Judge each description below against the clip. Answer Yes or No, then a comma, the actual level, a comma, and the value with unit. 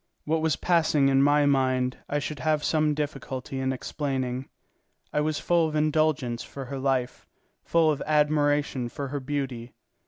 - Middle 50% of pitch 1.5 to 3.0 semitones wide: Yes, narrow, 2.5 semitones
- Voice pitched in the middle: Yes, medium, 145 Hz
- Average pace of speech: Yes, average, 160 wpm